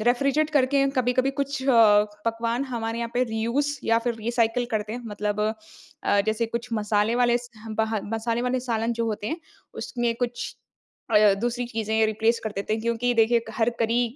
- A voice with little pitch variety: Yes, narrow, 1.8 semitones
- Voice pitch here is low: No, high, 235 Hz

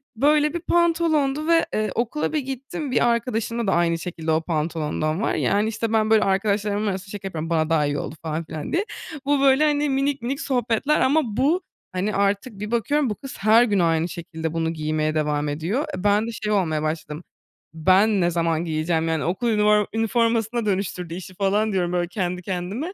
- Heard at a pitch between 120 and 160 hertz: No, high, 205 Hz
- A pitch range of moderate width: No, wide, 6.3 semitones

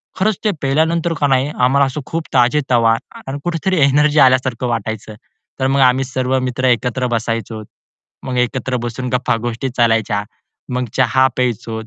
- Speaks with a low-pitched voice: Yes, low, 130 Hz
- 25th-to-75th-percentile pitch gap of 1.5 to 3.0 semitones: Yes, narrow, 2.5 semitones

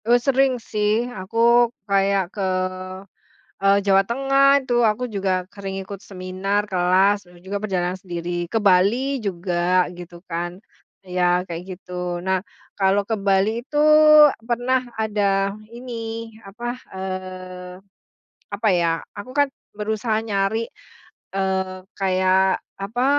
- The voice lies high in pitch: Yes, high, 195 Hz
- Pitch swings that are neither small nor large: Yes, average, 3.4 semitones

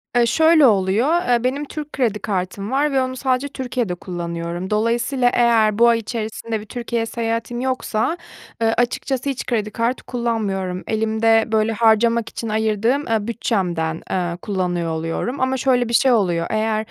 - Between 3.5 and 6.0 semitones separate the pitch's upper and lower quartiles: No, average, 3.1 semitones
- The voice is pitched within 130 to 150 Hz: No, high, 225 Hz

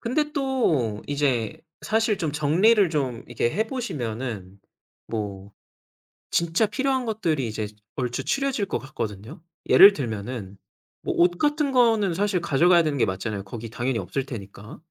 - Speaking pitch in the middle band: Yes, medium, 145 Hz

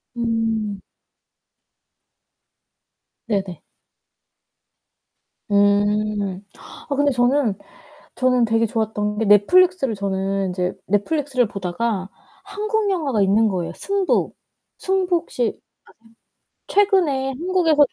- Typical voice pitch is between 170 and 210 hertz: No, high, 225 Hz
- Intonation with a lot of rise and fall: Yes, wide, 6.6 semitones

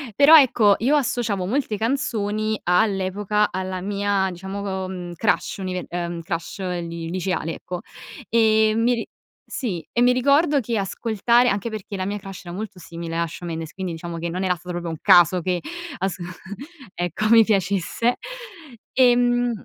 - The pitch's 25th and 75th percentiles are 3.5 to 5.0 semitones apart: Yes, average, 4.2 semitones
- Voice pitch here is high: Yes, high, 195 Hz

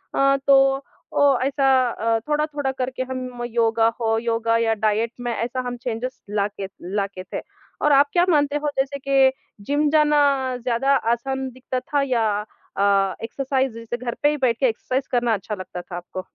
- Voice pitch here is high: Yes, very high, 255 Hz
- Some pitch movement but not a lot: Yes, average, 3.3 semitones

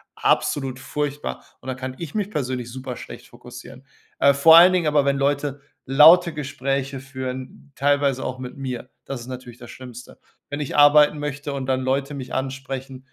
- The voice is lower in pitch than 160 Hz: Yes, low, 135 Hz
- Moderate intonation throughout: No, narrow, 2.0 semitones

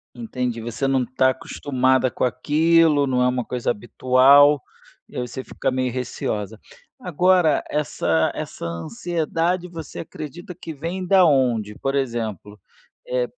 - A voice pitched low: Yes, low, 130 Hz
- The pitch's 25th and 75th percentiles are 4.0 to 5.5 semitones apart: Yes, average, 4.9 semitones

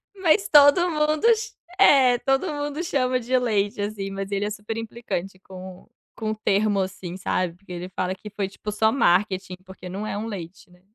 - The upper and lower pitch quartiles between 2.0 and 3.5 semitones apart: No, average, 5.3 semitones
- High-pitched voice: Yes, high, 210 Hz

